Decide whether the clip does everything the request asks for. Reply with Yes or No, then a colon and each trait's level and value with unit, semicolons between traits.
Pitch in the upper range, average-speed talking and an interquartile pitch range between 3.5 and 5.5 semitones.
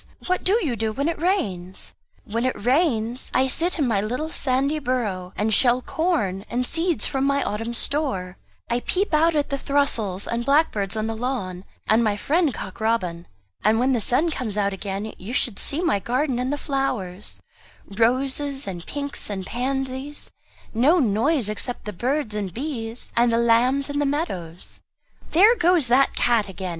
Yes: high, 245 Hz; average, 180 wpm; average, 5.2 semitones